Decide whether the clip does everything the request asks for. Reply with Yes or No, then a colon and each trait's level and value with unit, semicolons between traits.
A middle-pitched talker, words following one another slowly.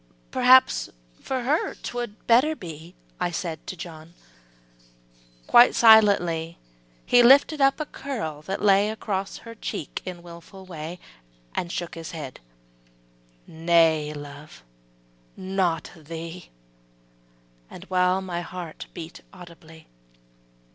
Yes: medium, 180 Hz; slow, 115 wpm